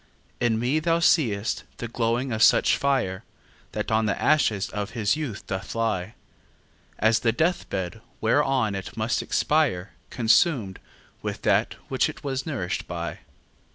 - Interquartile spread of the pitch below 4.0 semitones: No, average, 5.1 semitones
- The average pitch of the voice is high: No, low, 115 Hz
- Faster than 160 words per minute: No, average, 150 wpm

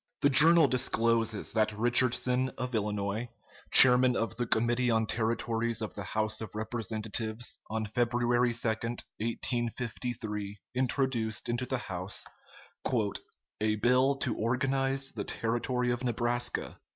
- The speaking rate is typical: No, slow, 125 wpm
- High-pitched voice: No, low, 120 Hz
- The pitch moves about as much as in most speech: No, narrow, 2.2 semitones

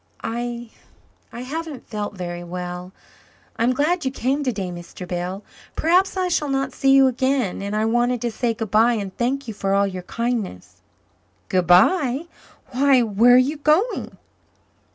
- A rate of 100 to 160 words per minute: Yes, average, 155 wpm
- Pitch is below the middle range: No, high, 240 Hz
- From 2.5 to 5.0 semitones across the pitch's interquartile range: No, wide, 5.6 semitones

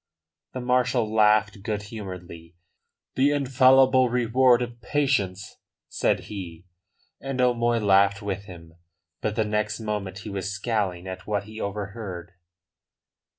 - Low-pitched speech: Yes, low, 105 Hz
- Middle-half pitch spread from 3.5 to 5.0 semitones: Yes, average, 3.9 semitones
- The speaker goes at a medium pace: No, slow, 125 wpm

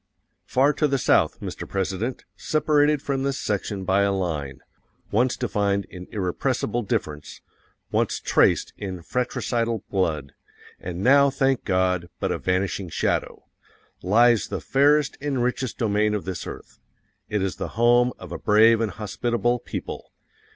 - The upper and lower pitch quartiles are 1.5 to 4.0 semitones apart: No, average, 5.1 semitones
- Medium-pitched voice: No, low, 110 Hz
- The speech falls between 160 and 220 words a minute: No, average, 145 wpm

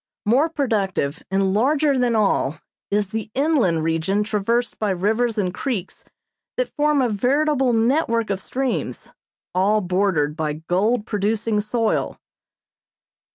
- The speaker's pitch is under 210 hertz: No, high, 215 Hz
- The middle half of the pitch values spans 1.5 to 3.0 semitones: No, average, 4.5 semitones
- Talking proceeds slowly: Yes, slow, 125 wpm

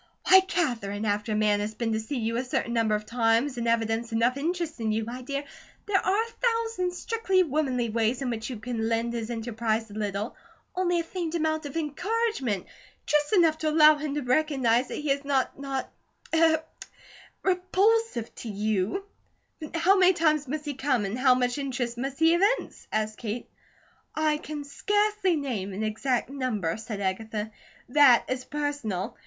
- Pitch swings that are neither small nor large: No, wide, 5.9 semitones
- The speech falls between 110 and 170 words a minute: No, average, 180 wpm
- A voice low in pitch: No, very high, 260 Hz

